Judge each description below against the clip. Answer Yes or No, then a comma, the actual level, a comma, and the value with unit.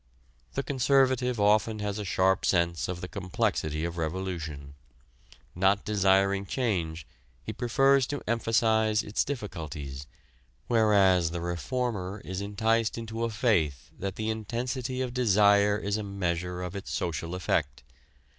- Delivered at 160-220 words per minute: No, slow, 135 wpm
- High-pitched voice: No, low, 100 Hz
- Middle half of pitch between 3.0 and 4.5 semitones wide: Yes, average, 4.2 semitones